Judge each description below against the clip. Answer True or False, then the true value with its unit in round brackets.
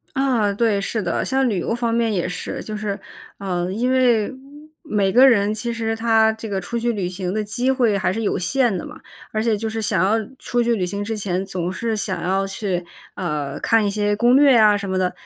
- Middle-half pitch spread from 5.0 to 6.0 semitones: False (3.3 semitones)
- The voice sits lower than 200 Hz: False (215 Hz)